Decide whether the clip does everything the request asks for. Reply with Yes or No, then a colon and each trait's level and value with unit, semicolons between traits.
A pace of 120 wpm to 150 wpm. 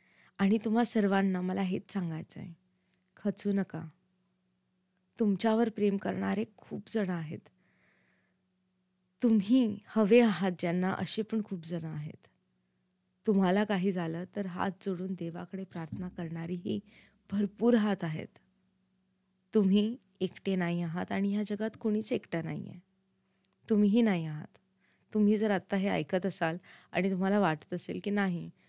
Yes: fast, 130 wpm